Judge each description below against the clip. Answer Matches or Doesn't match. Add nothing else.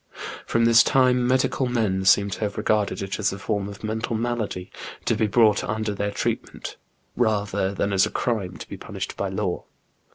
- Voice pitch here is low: Matches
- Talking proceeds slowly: Doesn't match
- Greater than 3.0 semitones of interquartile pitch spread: Doesn't match